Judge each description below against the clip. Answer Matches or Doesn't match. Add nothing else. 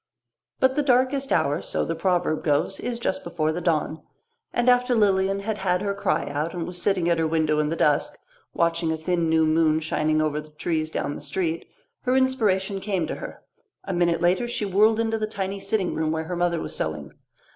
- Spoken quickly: Matches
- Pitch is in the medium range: Matches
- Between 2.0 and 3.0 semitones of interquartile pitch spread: Doesn't match